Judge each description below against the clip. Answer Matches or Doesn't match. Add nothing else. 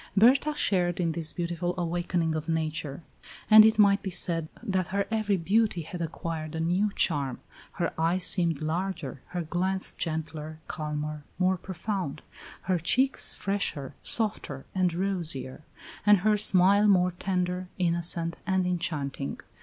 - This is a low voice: Doesn't match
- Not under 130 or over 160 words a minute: Matches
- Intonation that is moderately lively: Matches